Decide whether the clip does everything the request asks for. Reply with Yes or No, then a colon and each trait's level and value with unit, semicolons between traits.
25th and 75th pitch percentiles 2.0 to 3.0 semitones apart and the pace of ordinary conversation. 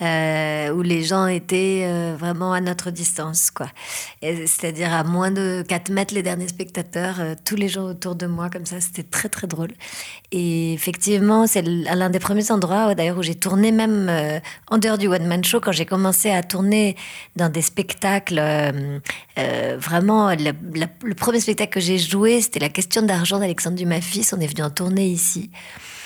Yes: average, 2.7 semitones; average, 195 wpm